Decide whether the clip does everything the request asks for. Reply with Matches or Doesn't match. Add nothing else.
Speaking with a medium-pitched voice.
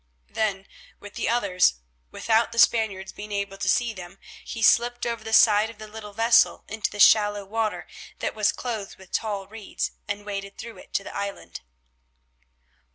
Doesn't match